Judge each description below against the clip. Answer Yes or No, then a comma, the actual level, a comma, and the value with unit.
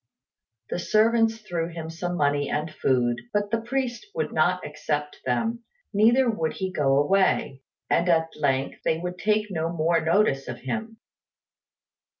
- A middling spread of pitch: No, wide, 6.3 semitones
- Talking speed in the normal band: Yes, average, 150 wpm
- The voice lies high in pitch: No, medium, 170 Hz